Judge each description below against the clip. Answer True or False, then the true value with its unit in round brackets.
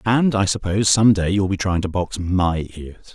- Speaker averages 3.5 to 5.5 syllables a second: True (4.8 syllables/s)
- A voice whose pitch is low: True (95 Hz)